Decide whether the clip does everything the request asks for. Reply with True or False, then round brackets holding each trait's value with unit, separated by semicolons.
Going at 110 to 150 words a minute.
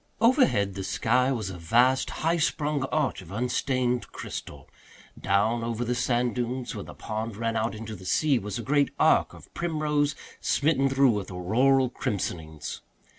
False (165 wpm)